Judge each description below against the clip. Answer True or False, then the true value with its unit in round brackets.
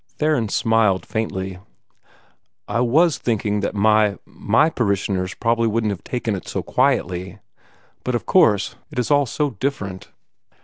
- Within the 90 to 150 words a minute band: True (135 wpm)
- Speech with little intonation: False (3.7 semitones)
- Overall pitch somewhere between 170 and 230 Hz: False (110 Hz)